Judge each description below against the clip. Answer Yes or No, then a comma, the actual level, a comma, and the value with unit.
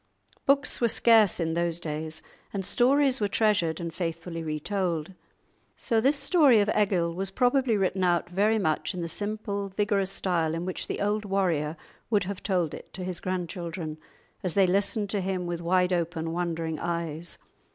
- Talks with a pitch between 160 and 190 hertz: Yes, medium, 185 Hz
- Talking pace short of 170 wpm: No, average, 175 wpm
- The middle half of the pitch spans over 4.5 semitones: No, average, 3.6 semitones